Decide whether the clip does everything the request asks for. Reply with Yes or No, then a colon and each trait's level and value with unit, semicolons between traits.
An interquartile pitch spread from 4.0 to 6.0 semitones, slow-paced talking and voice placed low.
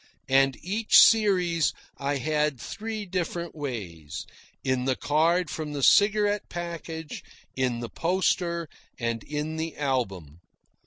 No: average, 5.1 semitones; slow, 120 wpm; medium, 155 Hz